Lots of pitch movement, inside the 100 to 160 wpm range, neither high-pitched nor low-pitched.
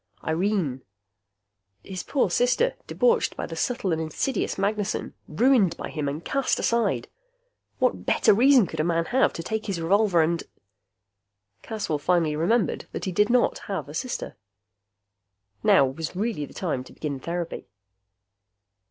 Yes: wide, 5.9 semitones; average, 150 wpm; medium, 180 Hz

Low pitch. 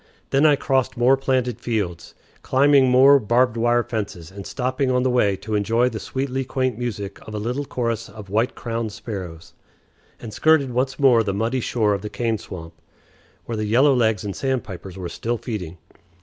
Yes: low, 120 Hz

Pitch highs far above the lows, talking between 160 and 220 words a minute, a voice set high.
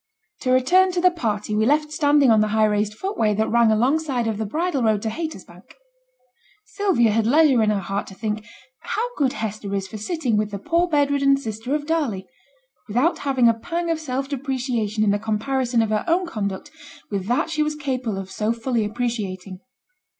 Yes: wide, 5.7 semitones; average, 200 wpm; high, 240 Hz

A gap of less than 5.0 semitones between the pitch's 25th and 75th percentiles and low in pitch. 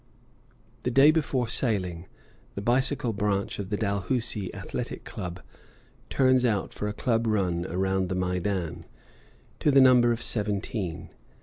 Yes: average, 4.6 semitones; low, 105 Hz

